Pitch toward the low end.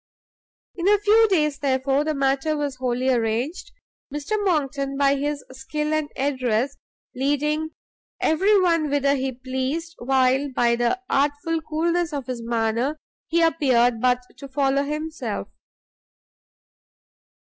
No: very high, 280 Hz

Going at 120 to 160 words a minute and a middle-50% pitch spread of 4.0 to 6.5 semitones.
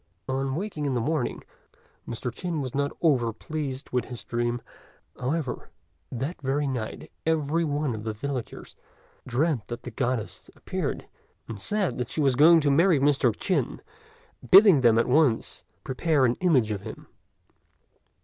Yes: average, 150 wpm; average, 4.4 semitones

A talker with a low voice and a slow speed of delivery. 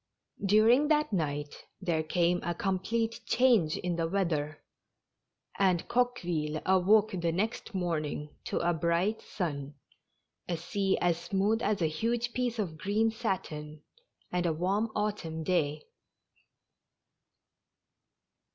No: medium, 180 Hz; slow, 125 wpm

